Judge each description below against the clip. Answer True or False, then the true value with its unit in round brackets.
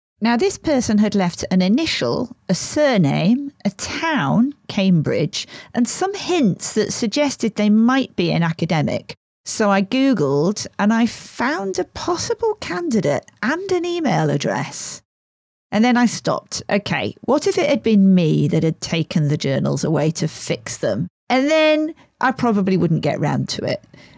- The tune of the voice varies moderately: False (7.8 semitones)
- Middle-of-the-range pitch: False (215 Hz)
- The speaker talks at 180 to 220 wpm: False (160 wpm)